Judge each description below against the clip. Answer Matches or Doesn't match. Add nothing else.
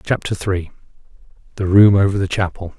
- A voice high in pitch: Doesn't match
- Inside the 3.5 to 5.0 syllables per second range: Doesn't match